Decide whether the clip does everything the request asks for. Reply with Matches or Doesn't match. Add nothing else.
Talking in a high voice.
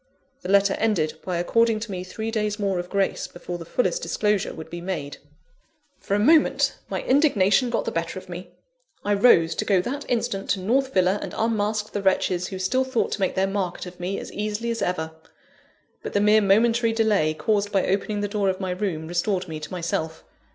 Matches